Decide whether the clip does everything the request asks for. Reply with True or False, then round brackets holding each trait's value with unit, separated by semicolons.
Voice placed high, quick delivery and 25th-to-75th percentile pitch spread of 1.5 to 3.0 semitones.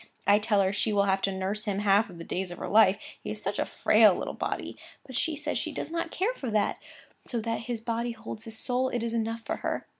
True (220 Hz; 260 wpm; 2.7 semitones)